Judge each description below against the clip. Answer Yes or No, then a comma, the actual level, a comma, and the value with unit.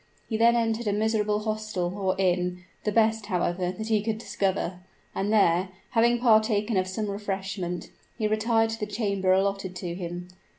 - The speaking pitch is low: No, high, 205 Hz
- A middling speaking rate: Yes, average, 170 wpm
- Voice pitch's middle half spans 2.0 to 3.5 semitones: Yes, average, 2.9 semitones